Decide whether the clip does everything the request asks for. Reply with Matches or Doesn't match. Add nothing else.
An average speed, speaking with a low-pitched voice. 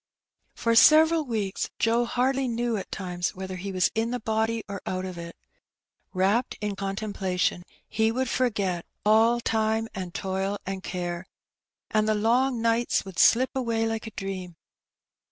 Doesn't match